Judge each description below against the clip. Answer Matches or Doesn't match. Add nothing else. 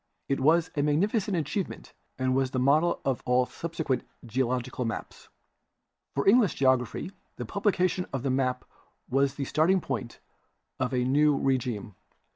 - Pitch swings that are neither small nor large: Matches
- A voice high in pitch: Doesn't match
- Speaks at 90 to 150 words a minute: Matches